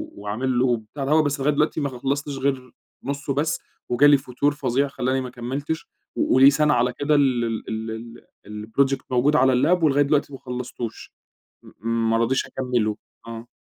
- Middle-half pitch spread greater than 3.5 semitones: No, average, 2.8 semitones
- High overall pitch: No, low, 130 Hz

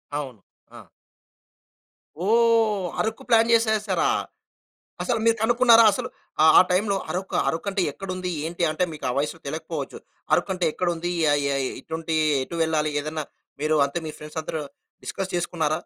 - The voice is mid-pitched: Yes, medium, 180 Hz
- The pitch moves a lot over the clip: Yes, wide, 5.9 semitones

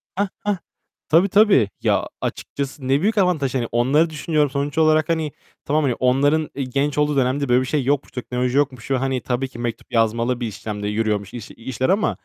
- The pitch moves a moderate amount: Yes, average, 3.7 semitones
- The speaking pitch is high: No, low, 135 Hz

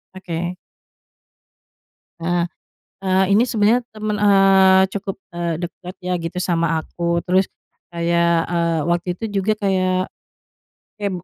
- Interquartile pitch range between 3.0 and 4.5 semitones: No, narrow, 2.4 semitones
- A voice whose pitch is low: No, medium, 185 Hz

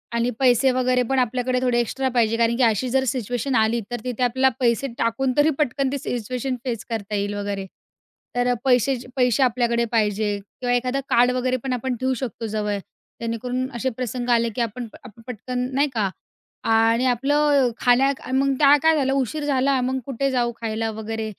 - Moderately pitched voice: No, high, 245 Hz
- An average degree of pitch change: No, narrow, 2.3 semitones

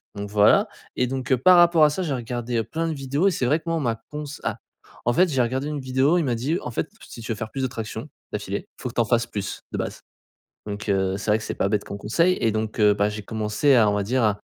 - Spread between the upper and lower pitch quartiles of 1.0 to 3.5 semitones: No, average, 5.0 semitones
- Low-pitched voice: Yes, low, 120 Hz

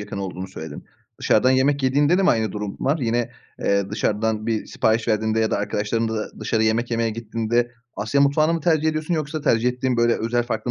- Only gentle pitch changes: No, average, 3.7 semitones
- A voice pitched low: Yes, low, 115 Hz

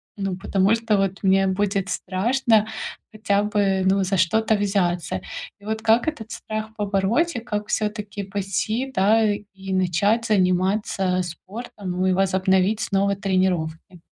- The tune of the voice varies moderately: No, narrow, 2.3 semitones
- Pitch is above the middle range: Yes, high, 200 Hz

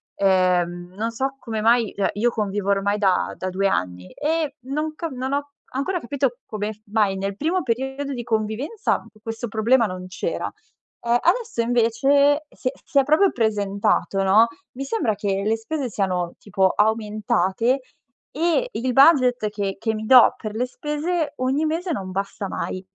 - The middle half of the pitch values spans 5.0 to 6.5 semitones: Yes, wide, 5.5 semitones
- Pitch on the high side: Yes, high, 230 Hz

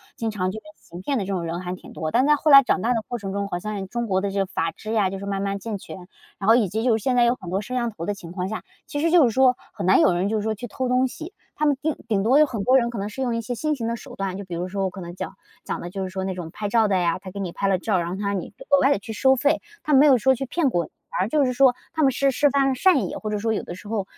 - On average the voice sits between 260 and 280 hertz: No, high, 215 Hz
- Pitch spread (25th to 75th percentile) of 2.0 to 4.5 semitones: No, average, 4.9 semitones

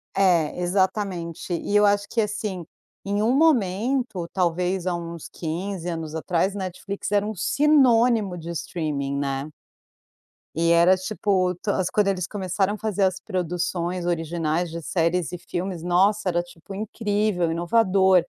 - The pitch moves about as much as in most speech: Yes, average, 3.1 semitones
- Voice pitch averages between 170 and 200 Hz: Yes, medium, 185 Hz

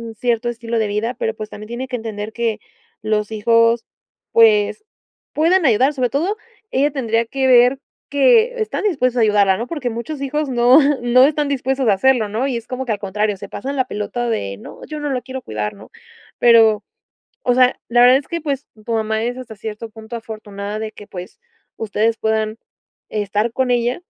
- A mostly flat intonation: No, average, 3.4 semitones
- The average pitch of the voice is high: Yes, high, 235 Hz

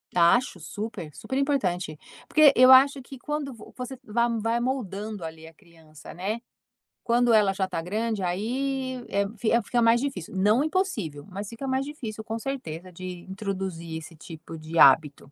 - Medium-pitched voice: No, high, 210 Hz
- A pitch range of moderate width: No, wide, 6.6 semitones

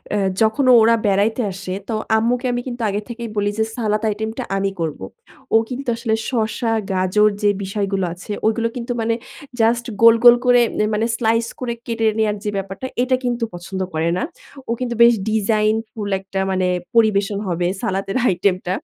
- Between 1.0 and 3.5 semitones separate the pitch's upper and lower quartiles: Yes, average, 3.0 semitones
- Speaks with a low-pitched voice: No, high, 220 Hz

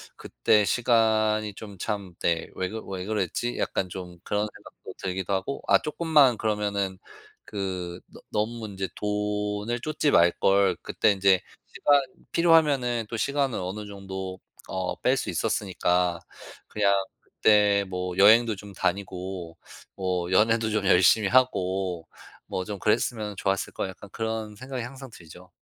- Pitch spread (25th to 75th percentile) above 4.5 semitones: No, average, 3.1 semitones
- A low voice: Yes, low, 105 Hz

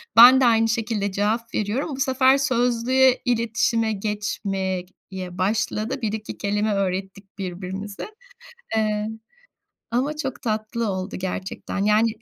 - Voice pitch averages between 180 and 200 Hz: No, high, 215 Hz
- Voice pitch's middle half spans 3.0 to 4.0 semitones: Yes, average, 3.3 semitones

